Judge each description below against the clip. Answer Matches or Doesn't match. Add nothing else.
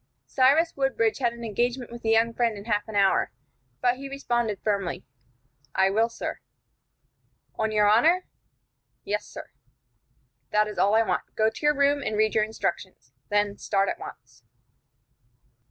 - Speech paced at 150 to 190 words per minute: Matches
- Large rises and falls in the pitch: Doesn't match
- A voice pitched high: Matches